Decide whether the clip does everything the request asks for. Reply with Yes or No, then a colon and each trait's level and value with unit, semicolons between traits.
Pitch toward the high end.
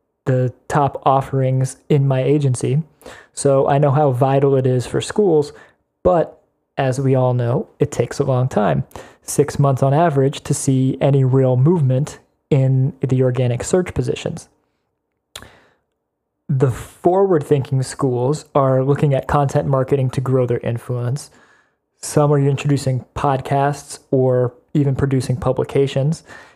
No: low, 135 Hz